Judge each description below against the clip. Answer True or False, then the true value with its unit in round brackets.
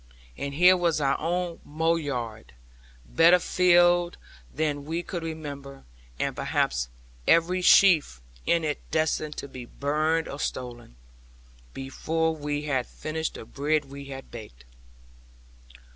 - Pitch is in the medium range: True (150 Hz)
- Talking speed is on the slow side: True (130 wpm)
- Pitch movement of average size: True (3.2 semitones)